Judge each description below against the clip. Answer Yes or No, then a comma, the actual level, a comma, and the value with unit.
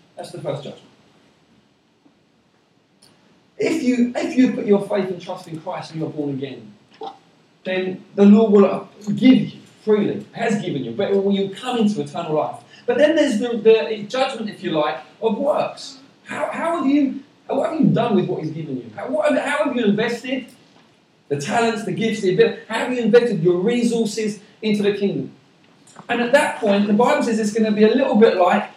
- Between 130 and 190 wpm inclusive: No, average, 200 wpm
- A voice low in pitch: No, high, 220 Hz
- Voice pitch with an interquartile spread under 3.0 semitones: No, average, 4.3 semitones